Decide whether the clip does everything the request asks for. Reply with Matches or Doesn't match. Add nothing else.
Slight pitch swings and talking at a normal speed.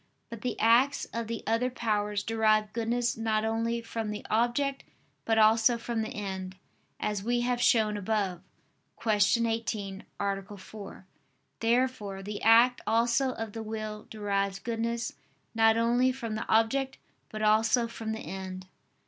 Matches